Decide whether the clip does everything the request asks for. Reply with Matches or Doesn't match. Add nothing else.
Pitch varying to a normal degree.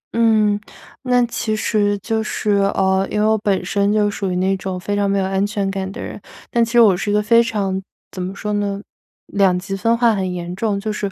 Doesn't match